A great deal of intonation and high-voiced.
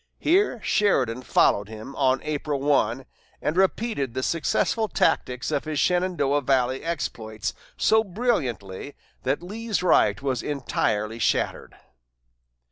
No: wide, 6.2 semitones; medium, 140 Hz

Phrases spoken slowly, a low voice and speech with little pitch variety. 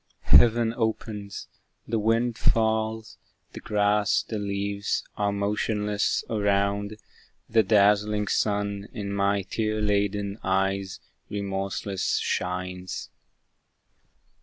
Yes: slow, 90 wpm; low, 105 Hz; narrow, 1.4 semitones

